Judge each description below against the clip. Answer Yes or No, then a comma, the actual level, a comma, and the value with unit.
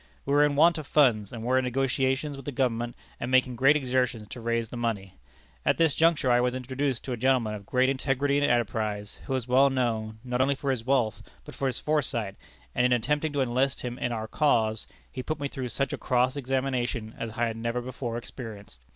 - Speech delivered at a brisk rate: Yes, fast, 225 wpm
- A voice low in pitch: Yes, low, 125 Hz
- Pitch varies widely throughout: No, average, 2.7 semitones